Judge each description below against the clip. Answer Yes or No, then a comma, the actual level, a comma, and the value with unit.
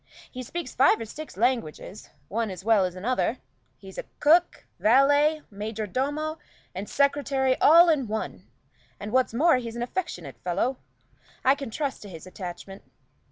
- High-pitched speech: Yes, high, 245 Hz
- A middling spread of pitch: No, wide, 5.7 semitones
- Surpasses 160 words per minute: No, average, 155 wpm